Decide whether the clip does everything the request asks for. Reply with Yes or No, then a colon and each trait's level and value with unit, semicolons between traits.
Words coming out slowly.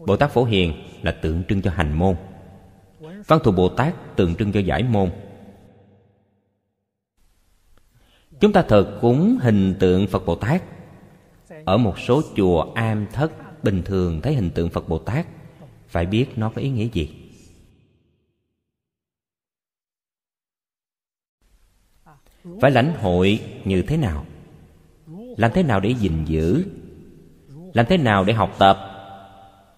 Yes: slow, 135 wpm